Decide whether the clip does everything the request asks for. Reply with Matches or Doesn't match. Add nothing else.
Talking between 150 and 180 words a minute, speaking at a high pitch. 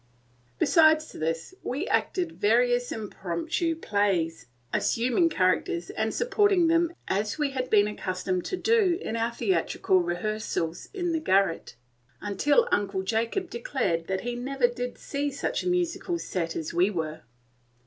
Doesn't match